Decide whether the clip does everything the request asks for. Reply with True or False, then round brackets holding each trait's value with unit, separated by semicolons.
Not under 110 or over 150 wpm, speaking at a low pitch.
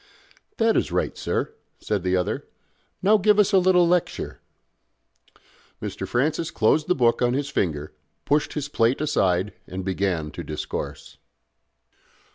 True (140 wpm; 130 Hz)